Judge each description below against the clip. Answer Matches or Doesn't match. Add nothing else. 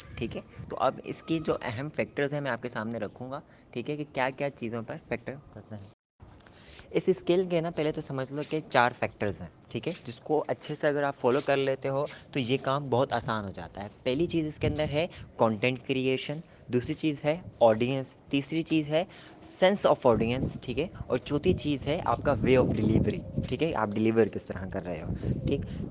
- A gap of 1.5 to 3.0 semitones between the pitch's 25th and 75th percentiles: Doesn't match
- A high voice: Doesn't match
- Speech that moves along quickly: Matches